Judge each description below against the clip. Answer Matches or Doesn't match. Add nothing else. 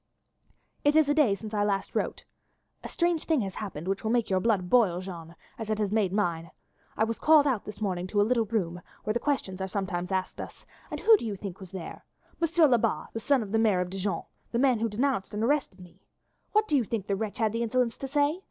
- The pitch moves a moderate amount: Matches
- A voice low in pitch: Doesn't match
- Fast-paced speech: Matches